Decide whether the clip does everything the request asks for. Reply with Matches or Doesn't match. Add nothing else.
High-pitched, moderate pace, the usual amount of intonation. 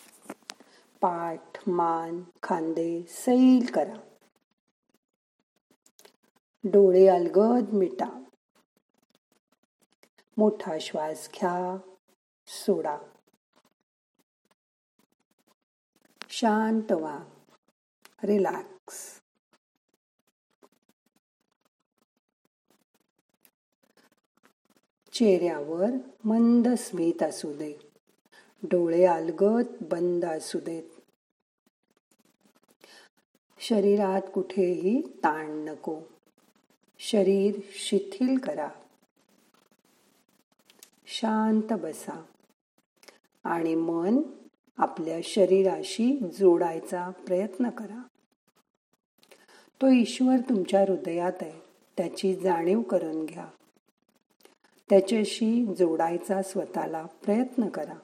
Doesn't match